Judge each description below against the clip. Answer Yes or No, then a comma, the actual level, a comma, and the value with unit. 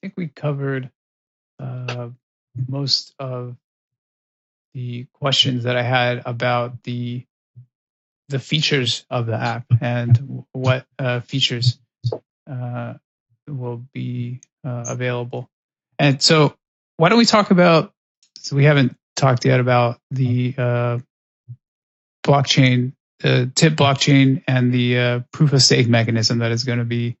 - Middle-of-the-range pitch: No, low, 125 Hz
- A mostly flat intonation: Yes, narrow, 2.1 semitones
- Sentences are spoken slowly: Yes, slow, 130 wpm